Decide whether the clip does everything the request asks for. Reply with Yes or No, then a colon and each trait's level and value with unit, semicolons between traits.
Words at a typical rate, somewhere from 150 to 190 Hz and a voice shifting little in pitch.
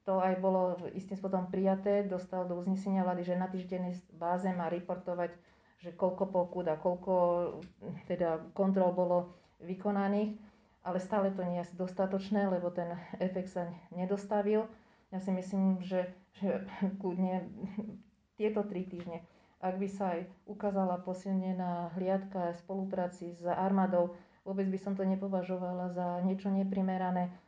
Yes: average, 140 wpm; medium, 185 Hz; narrow, 1.4 semitones